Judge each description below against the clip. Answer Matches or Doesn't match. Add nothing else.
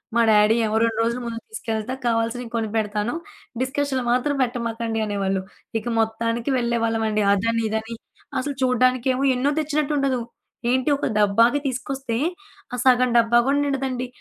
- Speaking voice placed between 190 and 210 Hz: Doesn't match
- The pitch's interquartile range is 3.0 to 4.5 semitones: Doesn't match